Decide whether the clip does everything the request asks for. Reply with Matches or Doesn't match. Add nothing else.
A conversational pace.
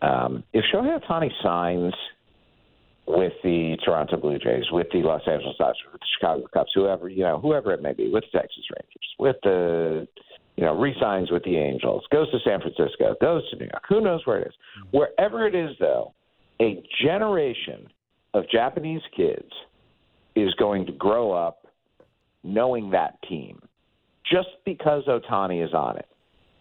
Matches